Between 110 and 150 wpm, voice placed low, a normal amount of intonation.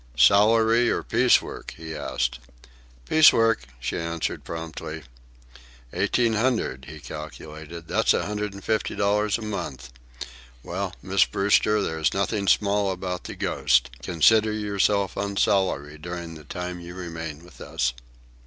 Yes: average, 145 wpm; very low, 90 Hz; average, 4.5 semitones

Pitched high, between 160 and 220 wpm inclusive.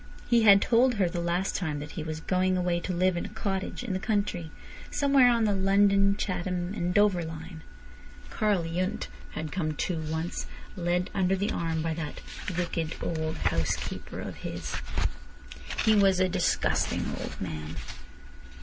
No: medium, 180 Hz; average, 165 wpm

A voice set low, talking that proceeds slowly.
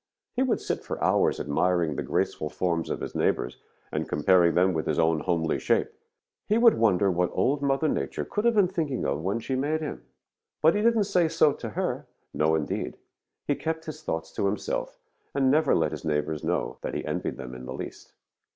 No: very low, 95 Hz; fast, 205 wpm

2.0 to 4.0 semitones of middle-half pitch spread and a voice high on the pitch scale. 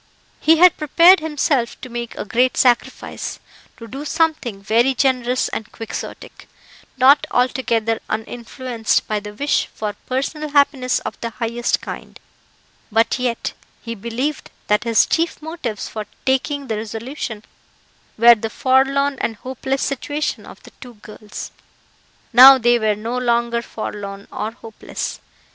Yes: average, 3.4 semitones; high, 245 Hz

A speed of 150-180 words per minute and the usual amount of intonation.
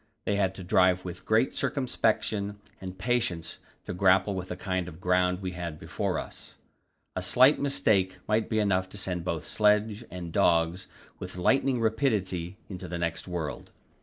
Yes: average, 165 wpm; average, 3.0 semitones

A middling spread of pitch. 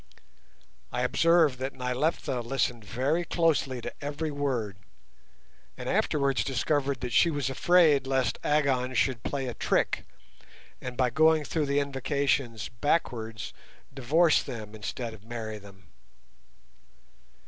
Yes: average, 3.5 semitones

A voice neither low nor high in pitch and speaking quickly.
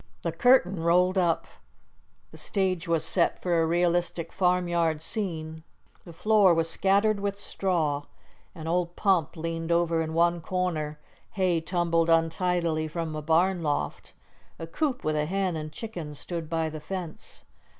No: medium, 170 Hz; average, 150 wpm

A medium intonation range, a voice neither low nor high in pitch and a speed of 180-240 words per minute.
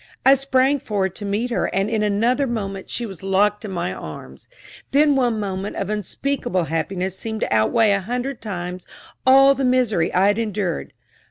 No: average, 4.6 semitones; high, 210 Hz; average, 185 wpm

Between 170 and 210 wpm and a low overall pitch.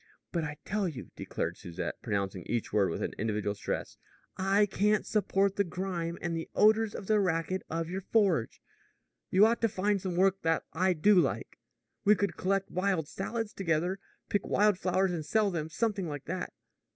No: average, 185 wpm; medium, 185 Hz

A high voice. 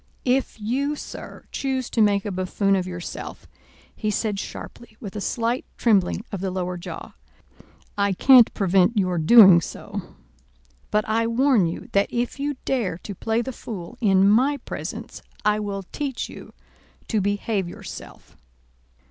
Yes: high, 210 Hz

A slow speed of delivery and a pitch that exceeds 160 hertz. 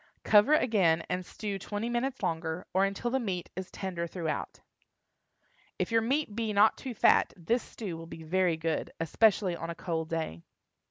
No: average, 175 wpm; high, 190 Hz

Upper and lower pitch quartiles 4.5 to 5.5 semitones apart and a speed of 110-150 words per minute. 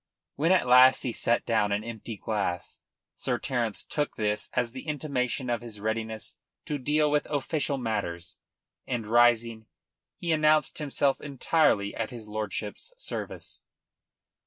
Yes: average, 4.8 semitones; average, 140 wpm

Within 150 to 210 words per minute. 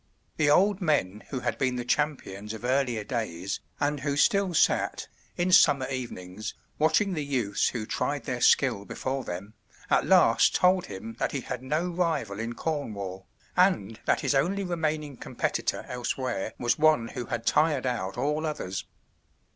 Yes: average, 165 wpm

